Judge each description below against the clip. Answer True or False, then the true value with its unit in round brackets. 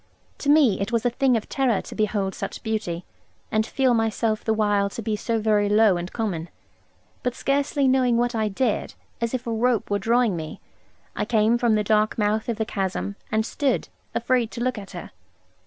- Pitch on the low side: False (220 Hz)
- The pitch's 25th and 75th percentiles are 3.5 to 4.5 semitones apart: False (2.7 semitones)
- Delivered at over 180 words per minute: True (205 wpm)